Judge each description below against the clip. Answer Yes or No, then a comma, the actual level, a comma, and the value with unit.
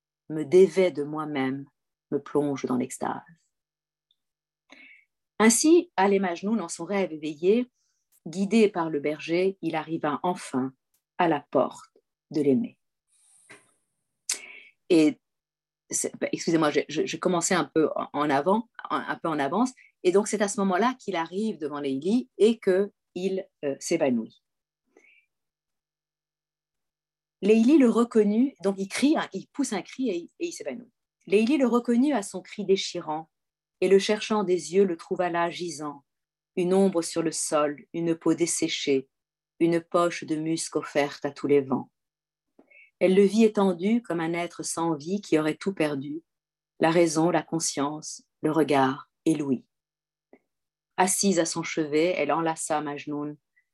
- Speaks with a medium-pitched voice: Yes, medium, 170 Hz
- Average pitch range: Yes, average, 4.6 semitones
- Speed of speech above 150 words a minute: No, slow, 145 wpm